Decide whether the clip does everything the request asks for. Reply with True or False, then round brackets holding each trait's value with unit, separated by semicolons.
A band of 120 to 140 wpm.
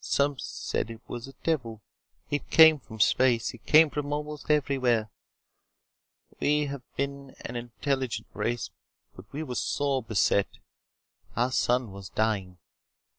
True (135 wpm)